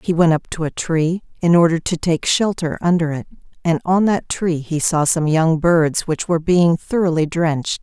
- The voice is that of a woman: Yes, female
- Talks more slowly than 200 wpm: No, fast, 205 wpm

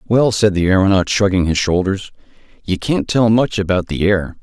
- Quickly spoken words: No, average, 190 wpm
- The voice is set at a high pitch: No, low, 100 Hz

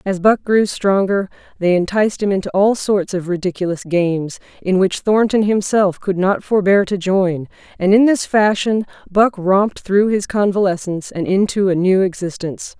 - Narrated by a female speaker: Yes, female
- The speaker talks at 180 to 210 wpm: No, average, 170 wpm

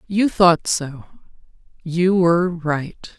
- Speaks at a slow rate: Yes, slow, 95 wpm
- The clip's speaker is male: No, female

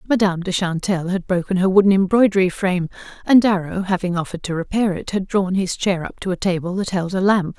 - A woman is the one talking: Yes, female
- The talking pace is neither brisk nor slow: No, fast, 220 wpm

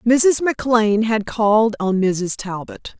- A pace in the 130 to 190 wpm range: Yes, average, 140 wpm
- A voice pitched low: No, high, 220 Hz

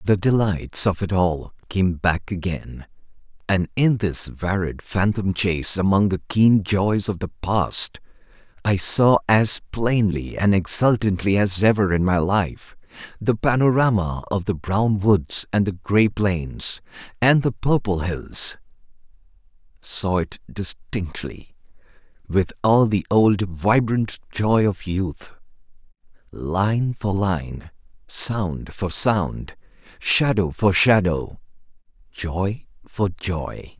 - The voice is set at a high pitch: No, low, 100 Hz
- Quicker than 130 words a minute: No, slow, 120 wpm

